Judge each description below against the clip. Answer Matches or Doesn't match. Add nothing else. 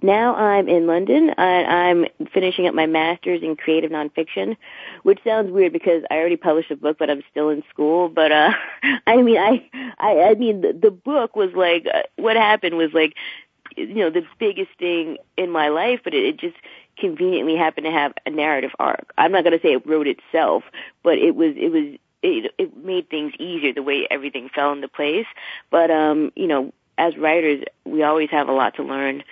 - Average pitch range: Doesn't match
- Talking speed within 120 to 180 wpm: Doesn't match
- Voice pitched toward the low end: Doesn't match